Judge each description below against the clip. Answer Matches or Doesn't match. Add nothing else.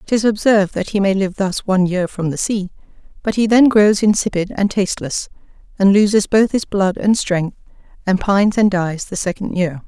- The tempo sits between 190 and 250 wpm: Matches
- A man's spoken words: Doesn't match